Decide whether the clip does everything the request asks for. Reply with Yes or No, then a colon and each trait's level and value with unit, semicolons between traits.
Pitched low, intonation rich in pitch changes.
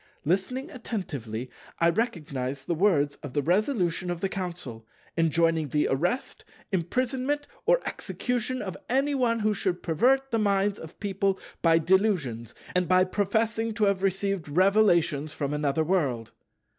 No: medium, 185 Hz; wide, 5.7 semitones